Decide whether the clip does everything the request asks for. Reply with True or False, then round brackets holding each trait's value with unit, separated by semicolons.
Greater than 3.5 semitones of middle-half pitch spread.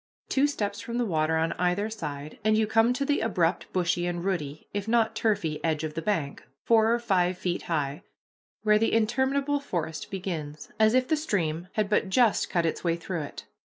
True (5.4 semitones)